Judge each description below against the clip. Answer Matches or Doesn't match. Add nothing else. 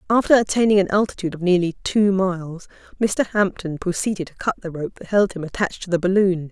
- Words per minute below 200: Doesn't match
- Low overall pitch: Doesn't match